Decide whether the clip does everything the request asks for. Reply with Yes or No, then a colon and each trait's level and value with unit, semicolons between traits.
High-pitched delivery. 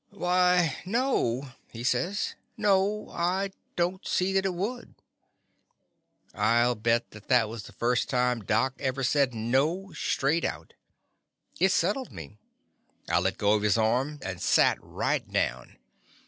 No: low, 135 Hz